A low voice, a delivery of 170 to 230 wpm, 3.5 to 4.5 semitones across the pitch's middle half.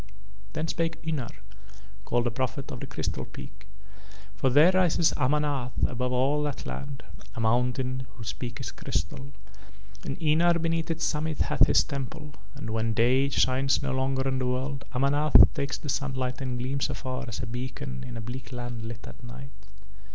No: low, 130 Hz; average, 175 wpm; average, 2.8 semitones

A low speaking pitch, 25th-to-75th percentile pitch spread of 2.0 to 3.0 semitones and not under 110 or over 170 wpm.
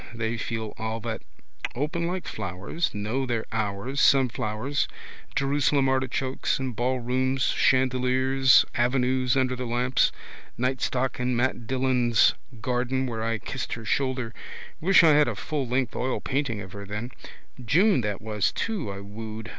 Yes: low, 125 Hz; average, 2.7 semitones; average, 140 wpm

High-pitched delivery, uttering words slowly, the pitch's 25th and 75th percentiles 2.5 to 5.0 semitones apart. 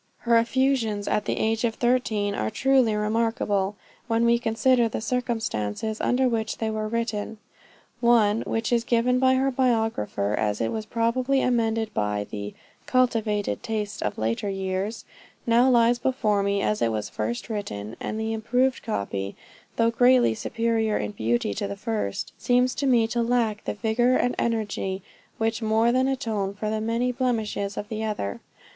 No: high, 225 Hz; average, 165 wpm; average, 2.8 semitones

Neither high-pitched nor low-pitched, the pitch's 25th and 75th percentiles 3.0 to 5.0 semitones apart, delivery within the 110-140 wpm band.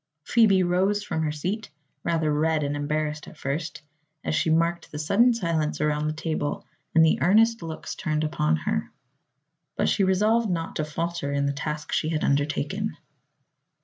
No: medium, 160 Hz; average, 3.5 semitones; average, 170 wpm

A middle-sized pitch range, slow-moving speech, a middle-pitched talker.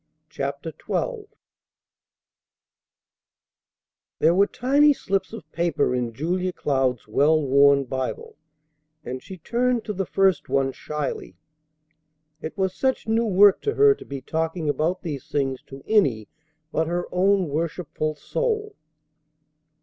No: wide, 6.6 semitones; slow, 125 wpm; medium, 165 Hz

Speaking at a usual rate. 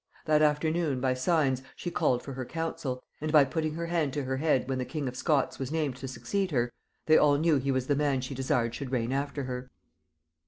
No: fast, 230 wpm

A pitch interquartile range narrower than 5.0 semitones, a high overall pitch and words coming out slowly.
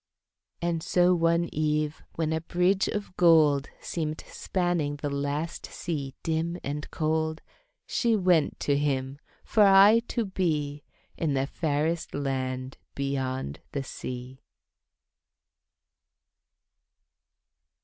No: average, 3.4 semitones; medium, 155 Hz; slow, 110 wpm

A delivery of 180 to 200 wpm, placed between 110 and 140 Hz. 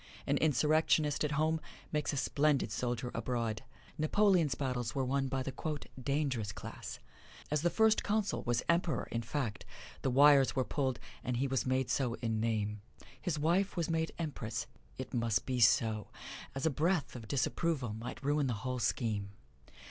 No: average, 165 wpm; low, 135 Hz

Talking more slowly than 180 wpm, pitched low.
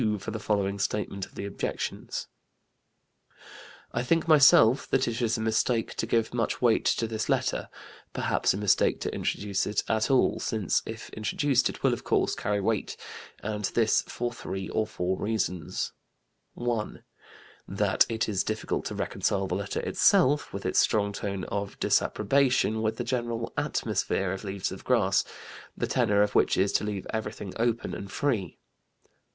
Yes: average, 165 wpm; low, 110 Hz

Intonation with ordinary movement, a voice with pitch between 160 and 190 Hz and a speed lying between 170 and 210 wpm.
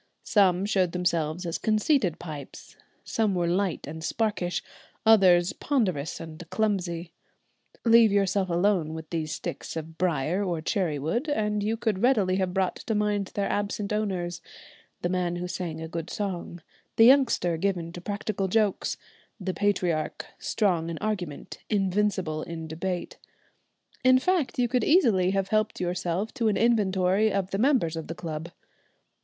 No: average, 3.6 semitones; medium, 185 Hz; average, 155 wpm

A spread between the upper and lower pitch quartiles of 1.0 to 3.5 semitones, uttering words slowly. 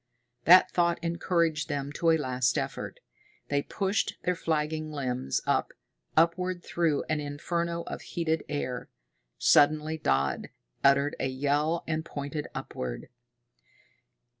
Yes: average, 3.0 semitones; slow, 120 wpm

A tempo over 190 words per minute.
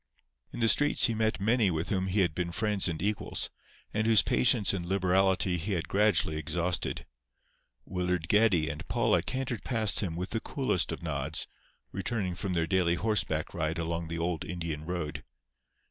No: average, 175 wpm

